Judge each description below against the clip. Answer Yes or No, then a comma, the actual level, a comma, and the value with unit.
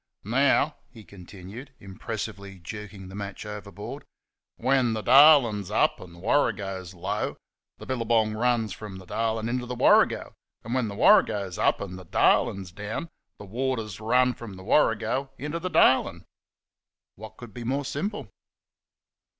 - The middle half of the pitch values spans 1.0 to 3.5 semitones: No, average, 4.1 semitones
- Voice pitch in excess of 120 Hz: No, low, 110 Hz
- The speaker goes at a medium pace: Yes, average, 160 wpm